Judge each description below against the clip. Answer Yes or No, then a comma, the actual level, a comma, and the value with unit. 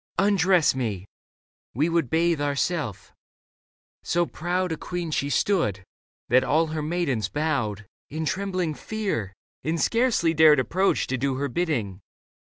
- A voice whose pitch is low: No, medium, 155 Hz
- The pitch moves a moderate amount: Yes, average, 5.0 semitones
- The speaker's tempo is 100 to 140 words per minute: Yes, slow, 135 wpm